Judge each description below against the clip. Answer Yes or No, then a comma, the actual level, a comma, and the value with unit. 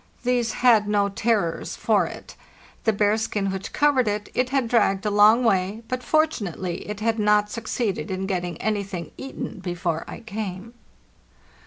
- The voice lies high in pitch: Yes, high, 210 Hz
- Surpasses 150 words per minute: Yes, average, 160 wpm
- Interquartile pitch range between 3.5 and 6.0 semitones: No, average, 3.1 semitones